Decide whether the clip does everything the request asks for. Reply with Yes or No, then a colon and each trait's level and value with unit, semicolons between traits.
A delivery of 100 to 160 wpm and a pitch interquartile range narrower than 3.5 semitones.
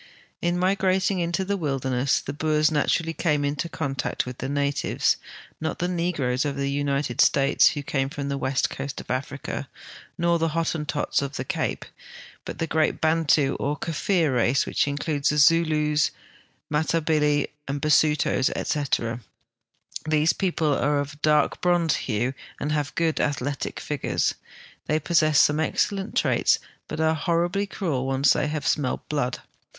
Yes: average, 155 wpm; average, 2.8 semitones